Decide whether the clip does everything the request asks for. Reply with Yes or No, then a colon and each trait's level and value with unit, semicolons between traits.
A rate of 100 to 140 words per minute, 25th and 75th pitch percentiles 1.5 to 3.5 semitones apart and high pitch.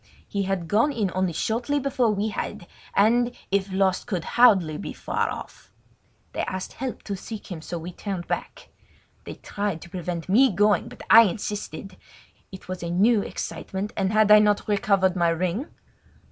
No: average, 175 wpm; average, 2.9 semitones; high, 200 Hz